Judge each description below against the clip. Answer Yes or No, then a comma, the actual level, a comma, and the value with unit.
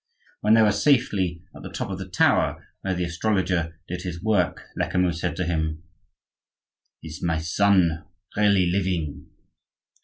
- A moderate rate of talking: Yes, average, 150 wpm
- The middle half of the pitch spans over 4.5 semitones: No, average, 2.9 semitones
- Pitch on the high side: No, very low, 90 Hz